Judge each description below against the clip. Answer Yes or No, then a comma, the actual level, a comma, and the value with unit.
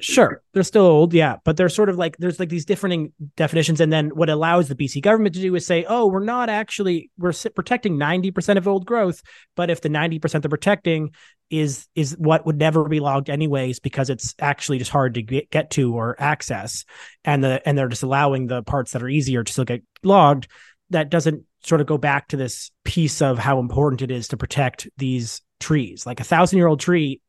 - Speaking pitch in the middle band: Yes, medium, 155 Hz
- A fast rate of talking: Yes, fast, 220 wpm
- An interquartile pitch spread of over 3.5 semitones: Yes, average, 4.2 semitones